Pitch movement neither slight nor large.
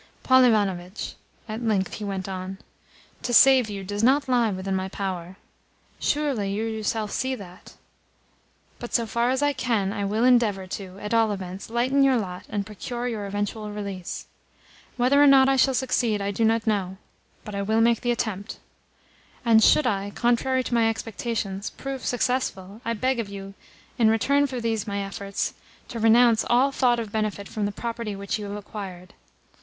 Yes: average, 3.4 semitones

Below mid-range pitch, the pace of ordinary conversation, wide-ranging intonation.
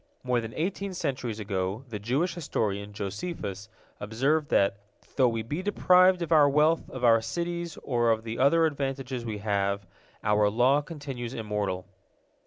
Yes: low, 120 Hz; average, 155 wpm; wide, 6.4 semitones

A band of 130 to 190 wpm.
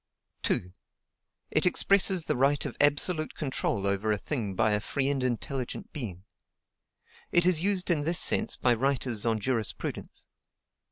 Yes: average, 150 wpm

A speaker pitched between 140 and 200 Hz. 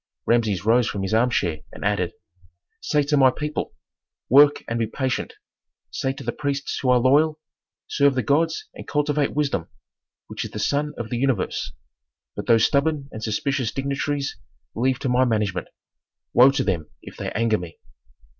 No: low, 130 Hz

